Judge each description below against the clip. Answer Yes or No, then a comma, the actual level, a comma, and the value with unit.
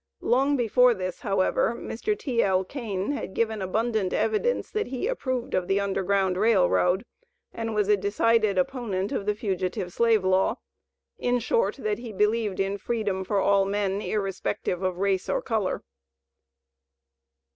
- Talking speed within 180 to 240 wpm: No, average, 150 wpm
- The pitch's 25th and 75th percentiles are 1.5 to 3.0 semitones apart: No, average, 3.5 semitones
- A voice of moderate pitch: No, high, 205 Hz